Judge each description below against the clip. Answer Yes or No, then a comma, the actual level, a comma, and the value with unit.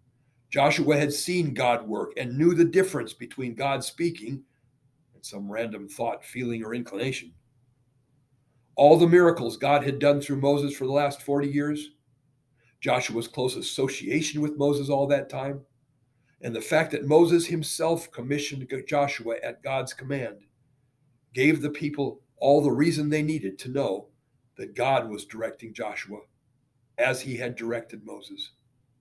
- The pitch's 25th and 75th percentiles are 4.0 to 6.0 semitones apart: No, average, 2.7 semitones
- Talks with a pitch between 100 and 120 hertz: No, low, 135 Hz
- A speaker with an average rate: Yes, average, 145 wpm